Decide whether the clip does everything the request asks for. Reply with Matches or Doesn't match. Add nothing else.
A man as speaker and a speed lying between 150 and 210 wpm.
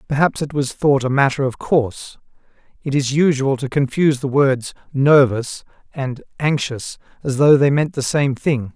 Matches